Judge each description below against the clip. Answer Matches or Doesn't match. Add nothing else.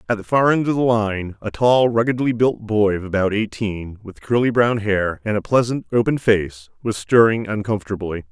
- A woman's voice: Doesn't match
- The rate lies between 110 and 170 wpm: Doesn't match